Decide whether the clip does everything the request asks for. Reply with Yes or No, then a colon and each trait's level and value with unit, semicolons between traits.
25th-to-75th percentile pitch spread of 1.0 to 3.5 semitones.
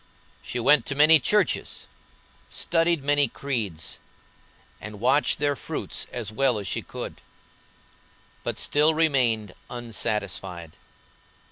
No: wide, 5.5 semitones